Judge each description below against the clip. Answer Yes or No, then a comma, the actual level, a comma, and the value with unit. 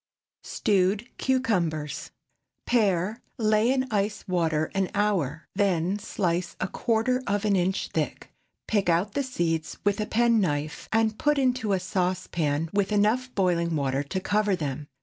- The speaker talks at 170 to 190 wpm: No, average, 145 wpm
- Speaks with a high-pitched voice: Yes, high, 195 Hz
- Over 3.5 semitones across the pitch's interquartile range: Yes, average, 4.3 semitones